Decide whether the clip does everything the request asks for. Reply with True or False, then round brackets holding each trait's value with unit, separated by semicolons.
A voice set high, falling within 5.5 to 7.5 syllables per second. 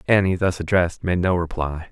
False (90 Hz; 5.8 syllables/s)